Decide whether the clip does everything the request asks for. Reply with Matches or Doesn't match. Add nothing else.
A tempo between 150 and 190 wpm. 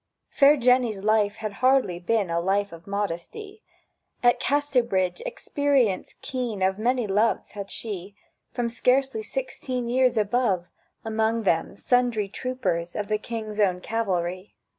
Doesn't match